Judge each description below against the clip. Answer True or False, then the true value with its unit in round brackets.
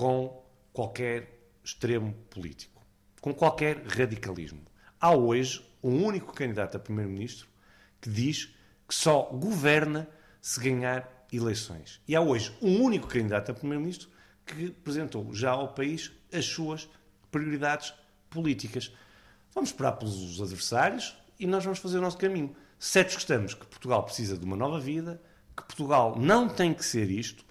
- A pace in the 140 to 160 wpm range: True (145 wpm)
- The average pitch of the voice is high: False (130 Hz)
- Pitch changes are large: True (6.9 semitones)